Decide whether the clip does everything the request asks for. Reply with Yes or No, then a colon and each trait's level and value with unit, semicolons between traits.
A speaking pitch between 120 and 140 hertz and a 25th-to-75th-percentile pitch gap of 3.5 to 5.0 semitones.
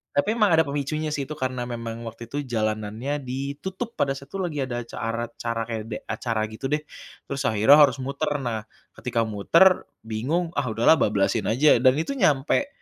Yes: low, 135 Hz; average, 4.6 semitones